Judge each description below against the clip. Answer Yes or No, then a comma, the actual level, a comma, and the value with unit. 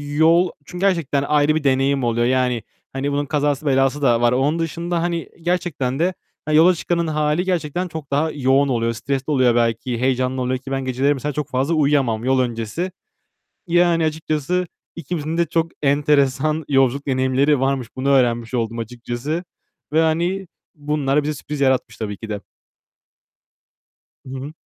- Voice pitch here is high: No, medium, 140 Hz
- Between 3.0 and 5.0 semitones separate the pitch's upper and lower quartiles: Yes, average, 3.5 semitones